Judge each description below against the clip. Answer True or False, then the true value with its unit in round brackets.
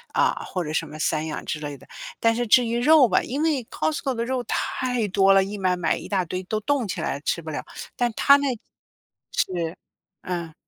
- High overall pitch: True (200 Hz)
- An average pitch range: False (6.6 semitones)